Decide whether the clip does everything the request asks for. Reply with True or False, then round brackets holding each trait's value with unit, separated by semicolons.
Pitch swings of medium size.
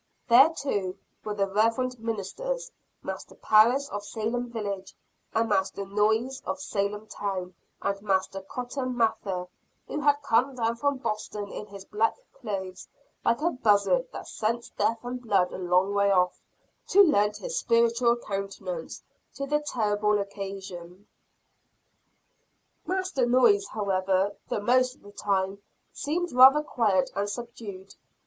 True (4.3 semitones)